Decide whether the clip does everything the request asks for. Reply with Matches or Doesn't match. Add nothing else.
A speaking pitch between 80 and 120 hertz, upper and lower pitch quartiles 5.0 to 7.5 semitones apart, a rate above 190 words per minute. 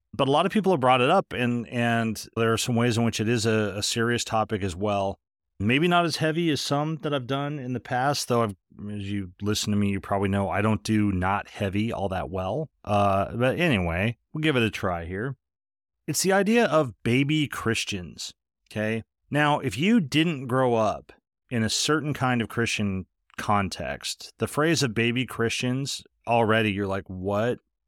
Matches